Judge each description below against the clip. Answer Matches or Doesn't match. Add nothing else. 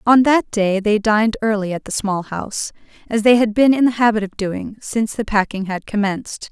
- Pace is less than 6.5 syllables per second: Matches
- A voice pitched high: Matches